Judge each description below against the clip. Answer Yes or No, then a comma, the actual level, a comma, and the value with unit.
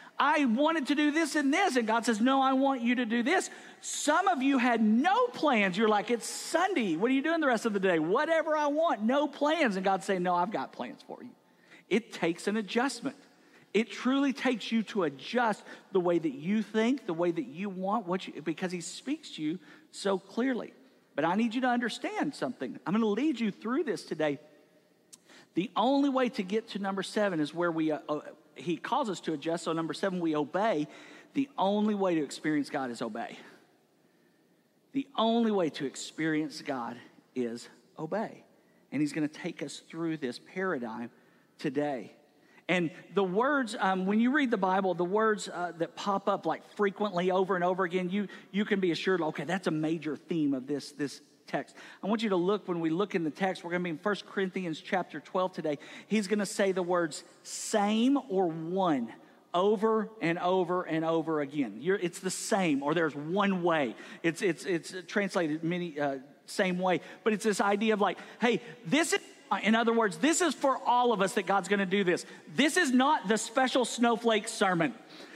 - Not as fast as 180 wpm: No, fast, 205 wpm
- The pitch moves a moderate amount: No, wide, 5.9 semitones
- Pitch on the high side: Yes, high, 200 Hz